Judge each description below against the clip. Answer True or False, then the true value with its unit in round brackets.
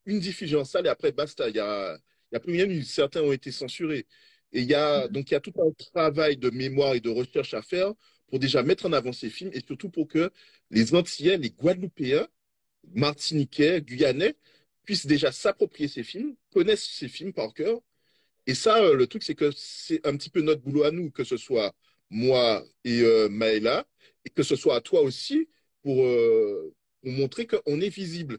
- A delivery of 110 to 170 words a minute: False (205 wpm)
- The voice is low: False (165 Hz)